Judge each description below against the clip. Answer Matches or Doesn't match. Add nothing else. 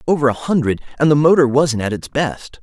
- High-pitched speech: Doesn't match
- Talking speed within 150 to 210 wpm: Doesn't match